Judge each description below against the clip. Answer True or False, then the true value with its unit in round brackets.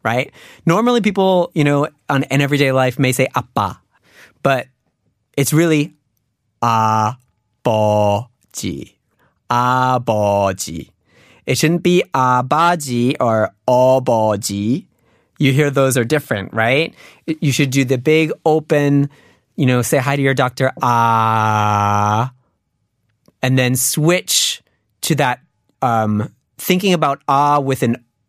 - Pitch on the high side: False (130 Hz)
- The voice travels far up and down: False (4.4 semitones)